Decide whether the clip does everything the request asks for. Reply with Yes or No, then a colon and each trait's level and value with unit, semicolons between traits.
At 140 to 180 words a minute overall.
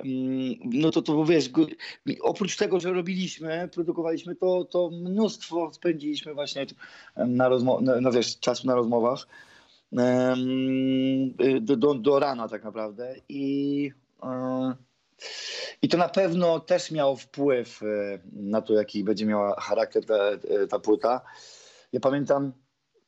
No: average, 120 wpm